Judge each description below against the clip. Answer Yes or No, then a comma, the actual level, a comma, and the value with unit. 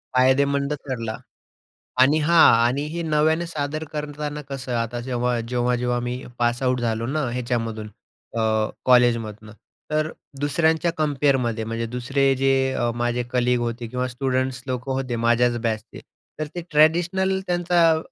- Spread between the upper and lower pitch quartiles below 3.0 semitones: No, average, 3.6 semitones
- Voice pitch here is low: Yes, low, 130 Hz